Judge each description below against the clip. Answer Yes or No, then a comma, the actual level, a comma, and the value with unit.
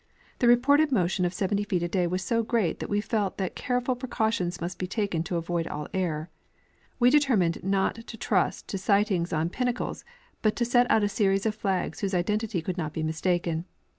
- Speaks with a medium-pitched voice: No, high, 195 Hz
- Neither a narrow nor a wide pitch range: Yes, average, 4.5 semitones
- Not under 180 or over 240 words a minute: Yes, fast, 205 wpm